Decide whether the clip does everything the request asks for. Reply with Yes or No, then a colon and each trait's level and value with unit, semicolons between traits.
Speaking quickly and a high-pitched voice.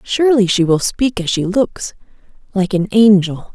No: average, 170 wpm; high, 200 Hz